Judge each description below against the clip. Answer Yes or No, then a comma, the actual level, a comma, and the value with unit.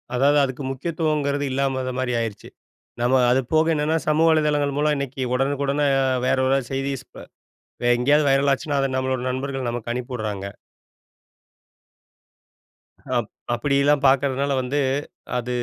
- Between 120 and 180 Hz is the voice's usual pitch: Yes, low, 135 Hz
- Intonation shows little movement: Yes, narrow, 2.1 semitones